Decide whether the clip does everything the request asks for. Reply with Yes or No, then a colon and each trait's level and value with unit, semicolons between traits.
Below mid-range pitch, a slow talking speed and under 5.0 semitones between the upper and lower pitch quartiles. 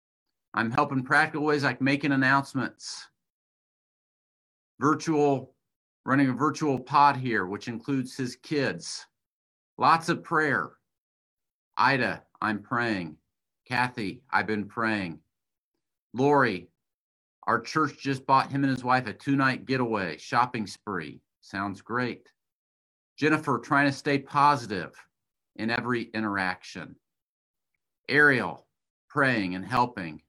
No: low, 125 Hz; slow, 110 wpm; wide, 5.4 semitones